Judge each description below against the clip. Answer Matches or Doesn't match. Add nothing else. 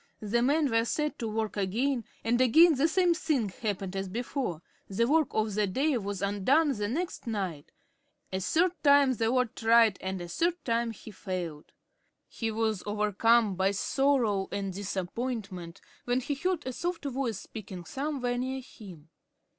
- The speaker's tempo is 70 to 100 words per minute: Doesn't match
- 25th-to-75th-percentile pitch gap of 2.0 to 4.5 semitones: Doesn't match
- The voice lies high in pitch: Matches